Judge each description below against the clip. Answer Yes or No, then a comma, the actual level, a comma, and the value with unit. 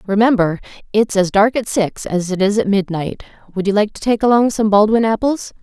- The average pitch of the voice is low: No, high, 205 Hz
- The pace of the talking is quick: Yes, fast, 215 wpm